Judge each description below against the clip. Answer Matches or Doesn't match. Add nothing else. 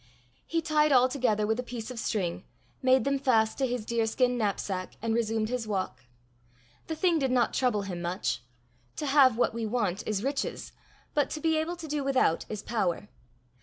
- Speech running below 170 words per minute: Doesn't match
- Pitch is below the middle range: Doesn't match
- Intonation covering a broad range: Doesn't match